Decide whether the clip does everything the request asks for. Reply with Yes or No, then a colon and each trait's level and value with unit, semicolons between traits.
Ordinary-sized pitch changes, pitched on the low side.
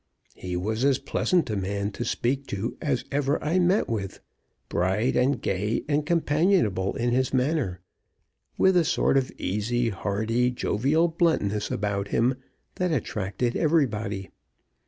No: wide, 6.2 semitones; low, 120 Hz